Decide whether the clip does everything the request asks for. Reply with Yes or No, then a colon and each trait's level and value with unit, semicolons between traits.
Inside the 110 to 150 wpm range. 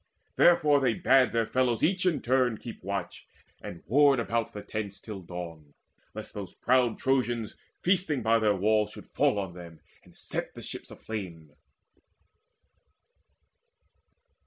Yes: average, 140 wpm